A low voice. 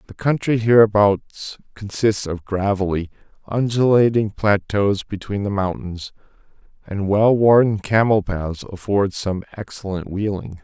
Yes: low, 100 Hz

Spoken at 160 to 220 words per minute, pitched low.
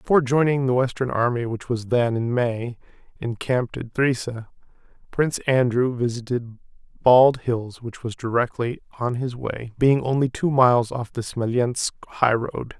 No: average, 150 wpm; low, 120 Hz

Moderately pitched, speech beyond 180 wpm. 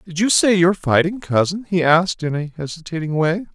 Yes: medium, 170 Hz; fast, 205 wpm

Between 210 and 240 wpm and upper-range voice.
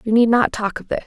No: fast, 335 wpm; high, 225 Hz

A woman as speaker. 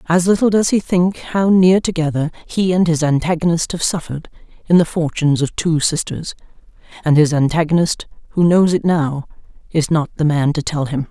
Yes: female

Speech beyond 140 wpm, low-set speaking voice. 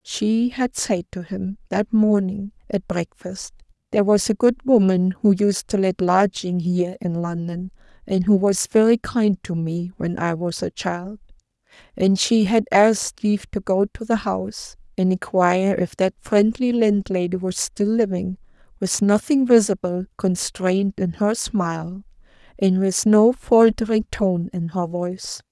No: average, 160 wpm; high, 195 Hz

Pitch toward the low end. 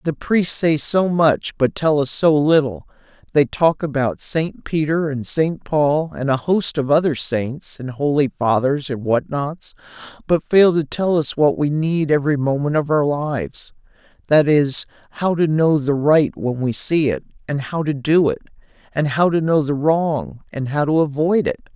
No: medium, 150 Hz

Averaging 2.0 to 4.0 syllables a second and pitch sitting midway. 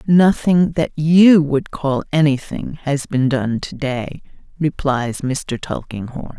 Yes: 3.4 syllables/s; medium, 145 Hz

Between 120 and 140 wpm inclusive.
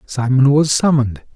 Yes: slow, 135 wpm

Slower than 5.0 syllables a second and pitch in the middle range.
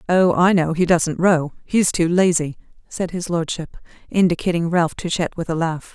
Yes: 4.7 syllables/s; medium, 170 Hz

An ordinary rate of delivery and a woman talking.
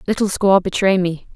Yes: average, 175 wpm; female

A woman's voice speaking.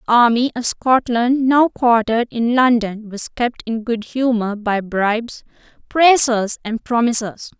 Yes: female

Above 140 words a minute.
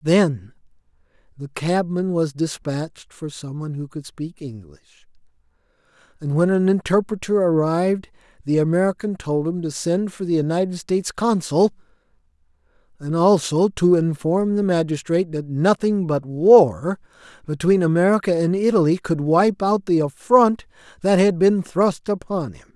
No: slow, 135 wpm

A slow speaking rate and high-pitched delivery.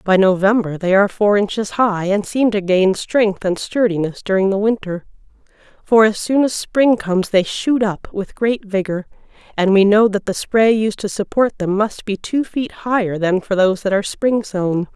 No: fast, 205 wpm; high, 205 Hz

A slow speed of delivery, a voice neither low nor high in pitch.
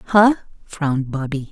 Yes: slow, 120 wpm; medium, 160 Hz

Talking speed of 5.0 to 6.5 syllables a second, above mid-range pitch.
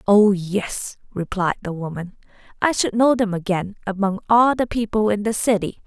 No: 4.8 syllables/s; high, 205 Hz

